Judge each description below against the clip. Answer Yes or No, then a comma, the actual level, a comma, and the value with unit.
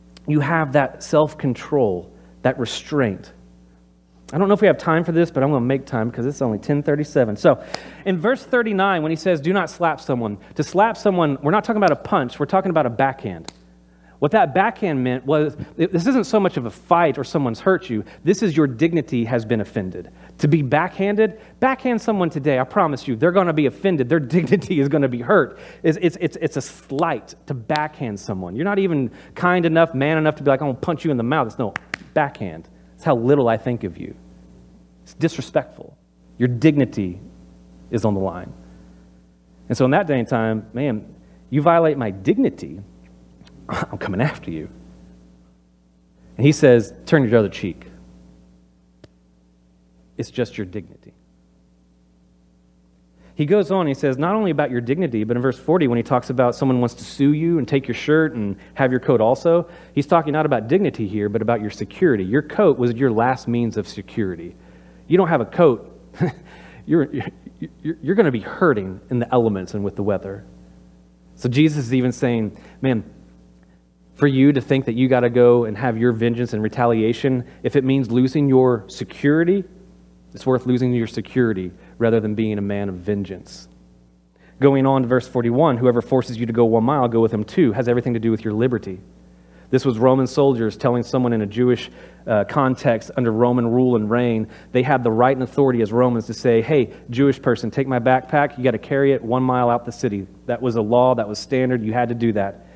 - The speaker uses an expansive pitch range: Yes, wide, 7.2 semitones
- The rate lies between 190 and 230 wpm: Yes, fast, 205 wpm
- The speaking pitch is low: Yes, low, 125 Hz